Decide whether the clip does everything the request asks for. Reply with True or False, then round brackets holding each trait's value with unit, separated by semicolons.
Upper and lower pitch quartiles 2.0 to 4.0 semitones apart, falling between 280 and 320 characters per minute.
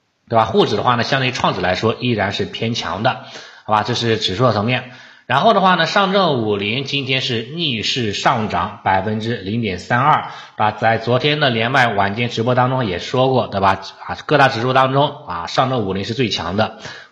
True (3.4 semitones; 300 characters per minute)